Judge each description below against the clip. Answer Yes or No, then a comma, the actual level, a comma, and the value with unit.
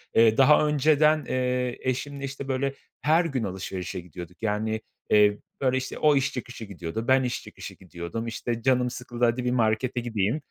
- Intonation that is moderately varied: Yes, average, 3.6 semitones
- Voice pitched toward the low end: Yes, low, 125 Hz